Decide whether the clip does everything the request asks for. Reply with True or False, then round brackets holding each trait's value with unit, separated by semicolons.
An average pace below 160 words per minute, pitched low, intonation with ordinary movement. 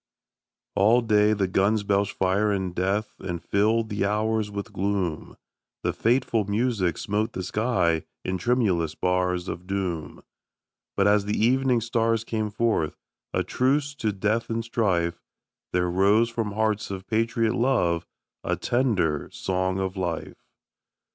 True (140 wpm; 105 Hz; 3.5 semitones)